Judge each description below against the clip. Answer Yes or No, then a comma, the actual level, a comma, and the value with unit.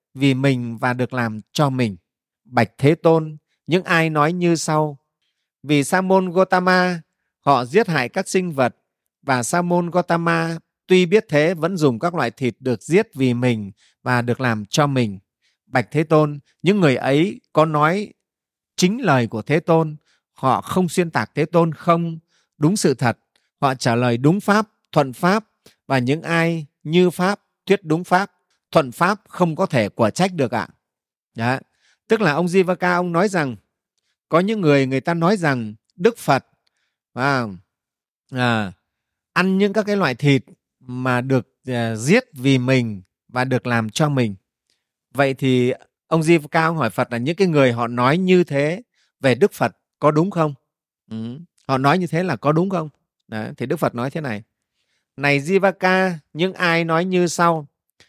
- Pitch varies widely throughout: Yes, wide, 5.8 semitones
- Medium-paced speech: Yes, average, 180 wpm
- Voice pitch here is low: No, medium, 150 Hz